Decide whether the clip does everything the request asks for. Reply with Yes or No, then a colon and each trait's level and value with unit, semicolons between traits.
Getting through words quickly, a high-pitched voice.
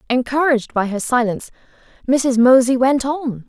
No: average, 140 wpm; very high, 255 Hz